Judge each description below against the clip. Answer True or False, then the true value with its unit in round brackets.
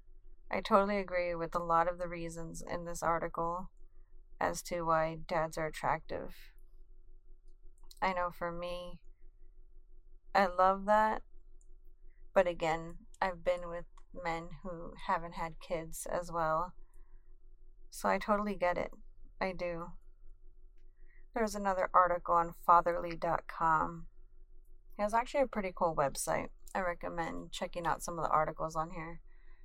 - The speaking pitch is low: False (175 Hz)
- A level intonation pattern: True (2.1 semitones)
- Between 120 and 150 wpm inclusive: True (135 wpm)